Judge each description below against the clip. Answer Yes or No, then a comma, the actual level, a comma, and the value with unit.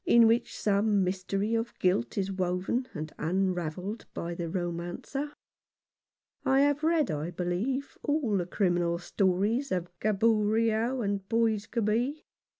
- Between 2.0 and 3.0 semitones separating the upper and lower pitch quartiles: No, average, 4.4 semitones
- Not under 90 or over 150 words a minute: Yes, average, 140 wpm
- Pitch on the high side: Yes, high, 200 Hz